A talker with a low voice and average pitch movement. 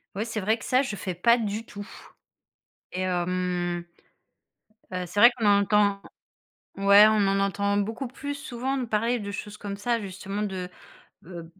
No: high, 205 Hz; average, 3.2 semitones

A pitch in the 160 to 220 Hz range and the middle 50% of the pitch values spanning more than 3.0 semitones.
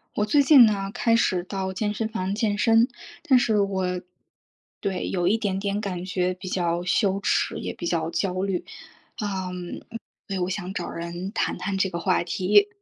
No: high, 190 Hz; narrow, 2.4 semitones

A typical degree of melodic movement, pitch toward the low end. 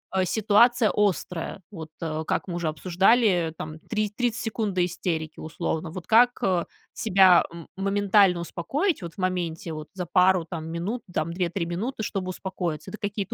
No: average, 3.5 semitones; medium, 185 Hz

